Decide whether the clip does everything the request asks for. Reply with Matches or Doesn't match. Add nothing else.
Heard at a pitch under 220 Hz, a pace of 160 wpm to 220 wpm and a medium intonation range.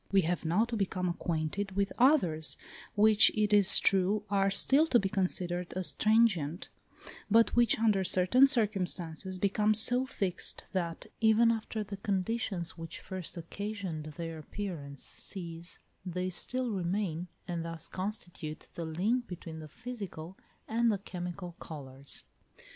Doesn't match